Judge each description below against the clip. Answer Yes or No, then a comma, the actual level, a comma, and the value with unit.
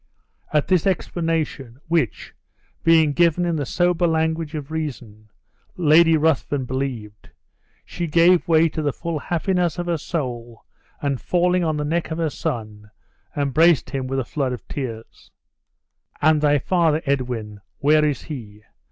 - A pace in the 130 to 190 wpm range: Yes, average, 150 wpm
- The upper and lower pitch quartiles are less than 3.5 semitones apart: No, average, 4.1 semitones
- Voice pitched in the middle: Yes, medium, 150 Hz